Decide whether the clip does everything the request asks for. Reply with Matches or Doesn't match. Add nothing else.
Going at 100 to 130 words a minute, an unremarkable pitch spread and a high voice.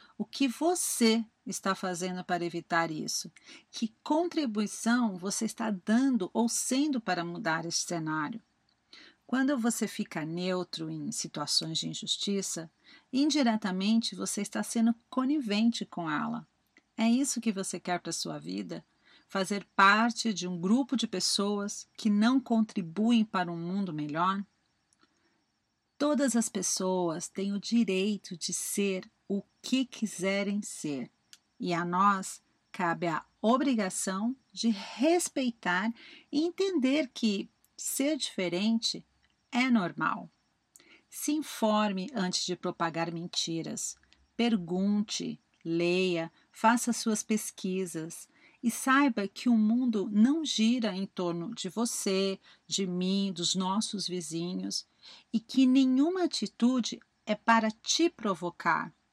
Matches